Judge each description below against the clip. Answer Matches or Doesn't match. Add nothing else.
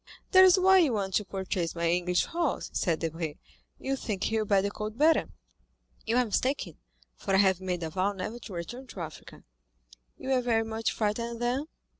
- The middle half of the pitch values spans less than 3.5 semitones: Doesn't match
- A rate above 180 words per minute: Matches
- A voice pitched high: Matches